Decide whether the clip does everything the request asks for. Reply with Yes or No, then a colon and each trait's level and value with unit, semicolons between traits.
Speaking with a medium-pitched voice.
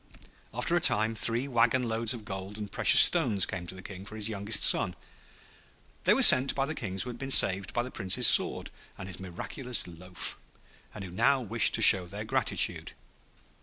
No: low, 105 Hz